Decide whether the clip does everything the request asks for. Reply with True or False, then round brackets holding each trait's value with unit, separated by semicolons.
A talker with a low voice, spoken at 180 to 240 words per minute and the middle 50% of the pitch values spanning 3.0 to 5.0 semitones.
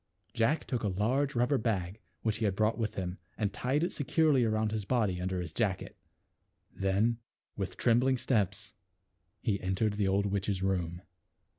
False (105 Hz; 165 wpm; 3.6 semitones)